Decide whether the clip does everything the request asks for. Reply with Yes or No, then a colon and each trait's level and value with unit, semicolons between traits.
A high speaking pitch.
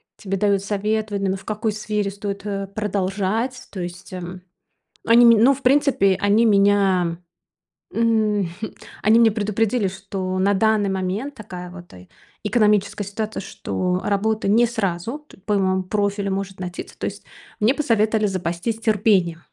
Yes: high, 205 Hz